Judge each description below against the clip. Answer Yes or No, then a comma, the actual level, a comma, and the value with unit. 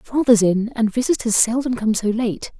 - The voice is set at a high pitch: Yes, high, 230 Hz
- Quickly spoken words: No, average, 185 wpm